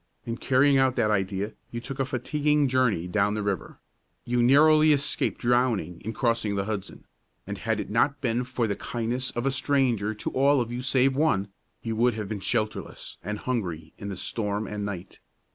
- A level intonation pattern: No, average, 4.0 semitones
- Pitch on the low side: Yes, low, 120 Hz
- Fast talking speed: No, average, 195 wpm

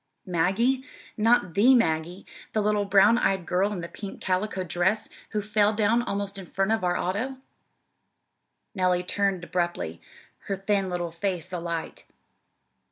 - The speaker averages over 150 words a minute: No, average, 145 wpm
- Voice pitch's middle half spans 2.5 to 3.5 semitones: Yes, average, 2.9 semitones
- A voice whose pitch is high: Yes, high, 195 Hz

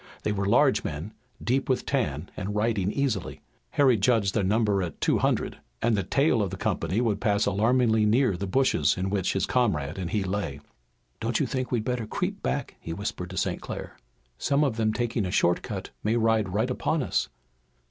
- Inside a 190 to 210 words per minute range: Yes, average, 200 wpm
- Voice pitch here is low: Yes, low, 105 Hz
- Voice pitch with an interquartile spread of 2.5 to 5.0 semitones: Yes, average, 4.0 semitones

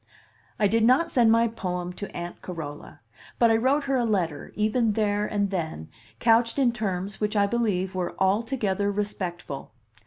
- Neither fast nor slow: Yes, average, 165 wpm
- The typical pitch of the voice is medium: No, high, 205 Hz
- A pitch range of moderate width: Yes, average, 3.8 semitones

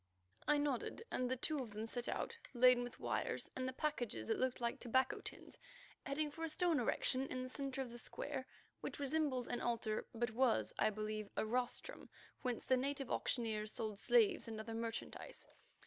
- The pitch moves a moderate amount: Yes, average, 3.3 semitones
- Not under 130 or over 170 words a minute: No, average, 190 wpm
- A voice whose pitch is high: Yes, very high, 250 Hz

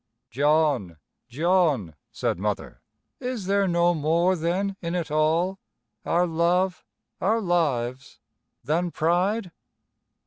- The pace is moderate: No, slow, 105 wpm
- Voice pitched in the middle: Yes, medium, 170 Hz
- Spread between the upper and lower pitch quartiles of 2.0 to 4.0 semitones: Yes, average, 3.3 semitones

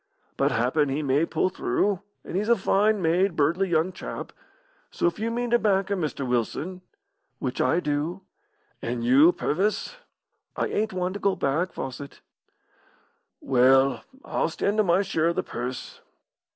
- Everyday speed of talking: Yes, average, 165 wpm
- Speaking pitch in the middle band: Yes, medium, 170 Hz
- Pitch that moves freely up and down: Yes, wide, 5.8 semitones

